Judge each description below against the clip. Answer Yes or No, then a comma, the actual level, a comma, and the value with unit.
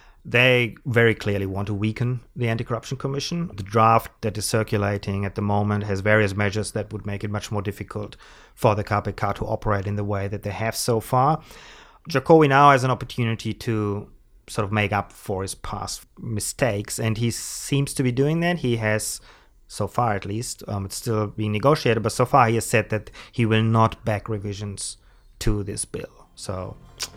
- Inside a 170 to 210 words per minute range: Yes, average, 200 wpm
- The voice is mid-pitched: No, low, 110 Hz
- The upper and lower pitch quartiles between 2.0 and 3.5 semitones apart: Yes, average, 2.8 semitones